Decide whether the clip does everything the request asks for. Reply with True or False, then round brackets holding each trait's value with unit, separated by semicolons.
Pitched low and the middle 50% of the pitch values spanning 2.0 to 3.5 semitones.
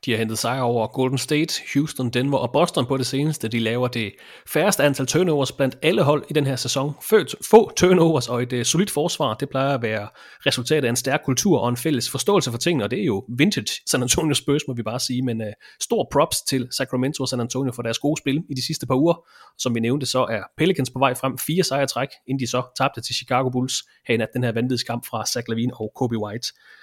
True (130 Hz; 3.2 semitones)